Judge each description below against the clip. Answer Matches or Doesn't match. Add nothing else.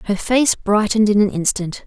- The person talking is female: Matches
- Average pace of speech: Matches